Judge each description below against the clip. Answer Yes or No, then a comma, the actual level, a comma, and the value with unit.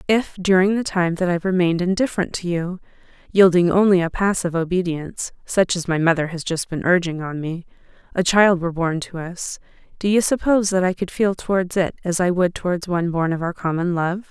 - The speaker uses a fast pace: Yes, fast, 210 wpm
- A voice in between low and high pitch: Yes, medium, 180 Hz